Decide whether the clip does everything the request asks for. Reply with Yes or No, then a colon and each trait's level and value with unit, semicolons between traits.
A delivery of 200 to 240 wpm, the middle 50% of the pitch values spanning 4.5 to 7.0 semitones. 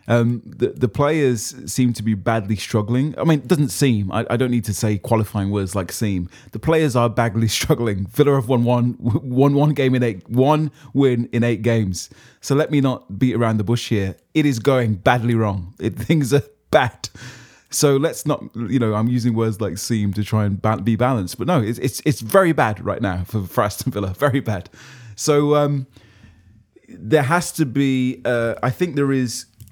No: fast, 205 wpm; average, 4.1 semitones